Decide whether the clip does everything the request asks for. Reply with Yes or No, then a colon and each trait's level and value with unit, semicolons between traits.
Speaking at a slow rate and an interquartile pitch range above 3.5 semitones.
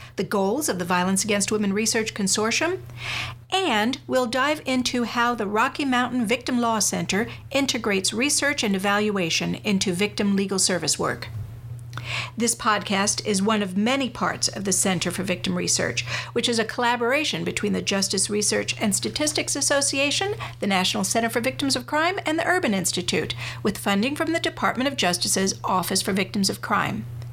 No: average, 165 wpm; average, 5.0 semitones